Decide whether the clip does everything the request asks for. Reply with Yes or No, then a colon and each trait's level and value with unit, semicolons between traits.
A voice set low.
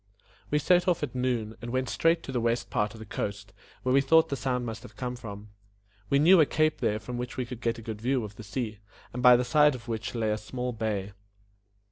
Yes: low, 120 Hz